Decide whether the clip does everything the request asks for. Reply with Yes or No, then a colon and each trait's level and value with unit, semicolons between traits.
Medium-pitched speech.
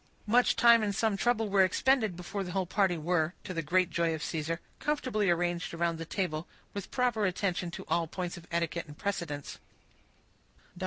Yes: medium, 180 Hz